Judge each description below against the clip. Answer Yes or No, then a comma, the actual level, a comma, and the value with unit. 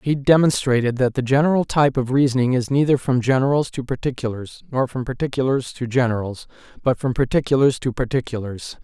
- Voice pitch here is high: No, low, 130 Hz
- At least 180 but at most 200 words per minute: No, average, 165 wpm